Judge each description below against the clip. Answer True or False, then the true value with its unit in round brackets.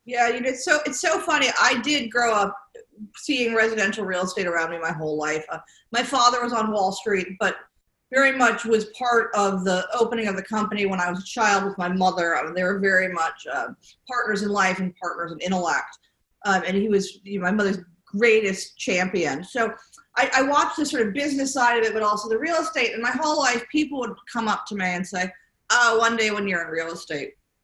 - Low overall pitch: False (215 Hz)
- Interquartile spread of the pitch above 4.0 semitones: True (4.5 semitones)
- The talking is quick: True (230 wpm)